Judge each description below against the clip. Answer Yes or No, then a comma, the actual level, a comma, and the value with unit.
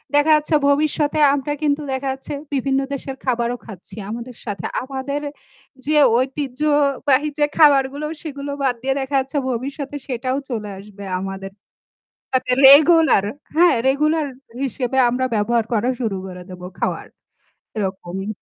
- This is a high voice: Yes, very high, 265 Hz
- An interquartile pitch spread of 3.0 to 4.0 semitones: Yes, average, 3.6 semitones